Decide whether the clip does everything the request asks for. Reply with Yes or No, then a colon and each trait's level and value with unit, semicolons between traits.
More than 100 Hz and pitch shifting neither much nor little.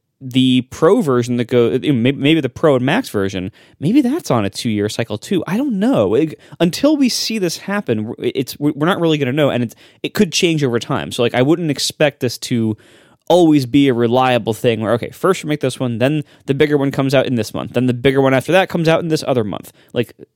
Yes: low, 135 Hz; average, 4.9 semitones